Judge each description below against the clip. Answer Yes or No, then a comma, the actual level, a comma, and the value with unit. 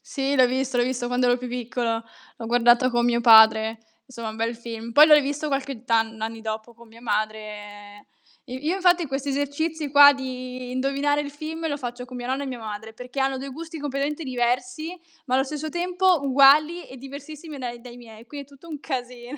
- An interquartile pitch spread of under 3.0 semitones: No, average, 3.3 semitones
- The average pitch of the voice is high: Yes, very high, 255 Hz